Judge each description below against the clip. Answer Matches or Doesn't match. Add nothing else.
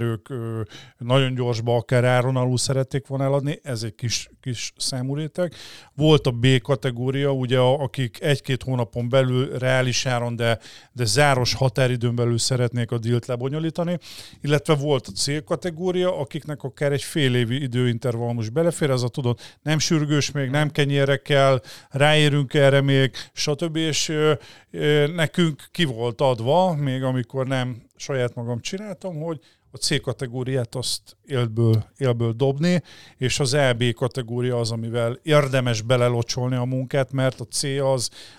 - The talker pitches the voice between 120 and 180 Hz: Matches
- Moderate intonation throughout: Matches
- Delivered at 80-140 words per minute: Doesn't match